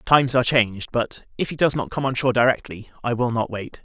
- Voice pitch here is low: Yes, low, 125 Hz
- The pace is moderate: No, fast, 250 wpm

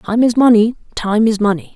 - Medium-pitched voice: No, high, 220 Hz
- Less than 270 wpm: Yes, fast, 205 wpm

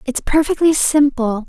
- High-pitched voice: Yes, very high, 280 Hz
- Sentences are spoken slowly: Yes, slow, 120 wpm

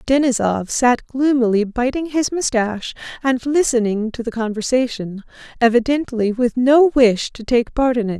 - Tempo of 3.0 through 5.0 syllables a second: Yes, 4.6 syllables/s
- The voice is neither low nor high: No, high, 245 Hz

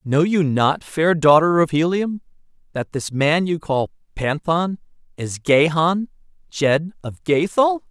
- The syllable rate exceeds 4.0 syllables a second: No, 3.8 syllables/s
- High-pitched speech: No, medium, 165 Hz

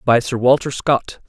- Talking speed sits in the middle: Yes, average, 190 wpm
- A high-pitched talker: No, low, 125 Hz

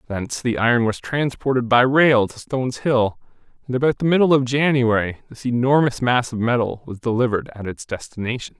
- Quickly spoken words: No, average, 180 wpm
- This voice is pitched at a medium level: No, low, 120 Hz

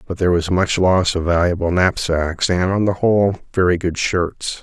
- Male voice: Yes, male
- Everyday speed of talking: Yes, average, 195 wpm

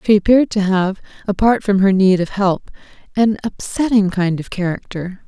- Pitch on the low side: No, high, 200 Hz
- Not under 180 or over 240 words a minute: No, average, 170 wpm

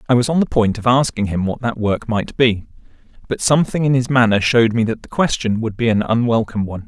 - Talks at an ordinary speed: No, fast, 245 wpm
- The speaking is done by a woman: No, male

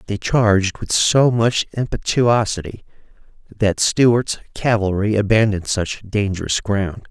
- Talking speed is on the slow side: Yes, slow, 110 wpm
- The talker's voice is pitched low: Yes, low, 105 Hz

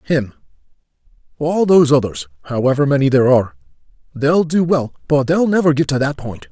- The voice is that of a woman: No, male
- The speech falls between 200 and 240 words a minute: No, average, 155 wpm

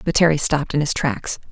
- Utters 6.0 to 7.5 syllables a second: Yes, 6.1 syllables/s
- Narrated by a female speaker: Yes, female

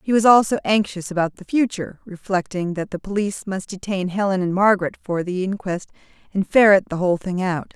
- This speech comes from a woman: Yes, female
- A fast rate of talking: No, average, 195 wpm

